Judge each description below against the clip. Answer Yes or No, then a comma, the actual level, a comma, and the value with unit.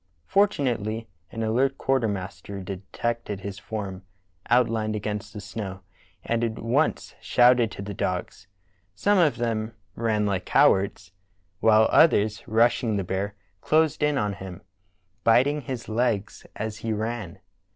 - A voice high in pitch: No, low, 110 Hz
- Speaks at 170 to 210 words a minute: No, slow, 135 wpm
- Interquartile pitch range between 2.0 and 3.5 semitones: Yes, average, 2.9 semitones